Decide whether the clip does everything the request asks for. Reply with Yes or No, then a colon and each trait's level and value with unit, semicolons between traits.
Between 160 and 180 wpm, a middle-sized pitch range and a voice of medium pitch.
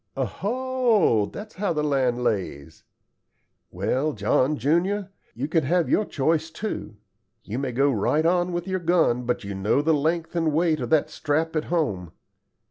No: average, 165 wpm; wide, 5.8 semitones; medium, 155 Hz